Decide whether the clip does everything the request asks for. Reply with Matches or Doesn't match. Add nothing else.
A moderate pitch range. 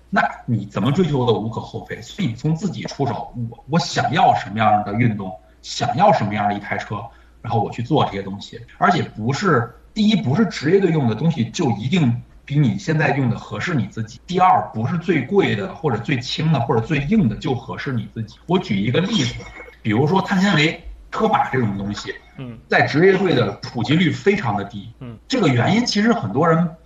Doesn't match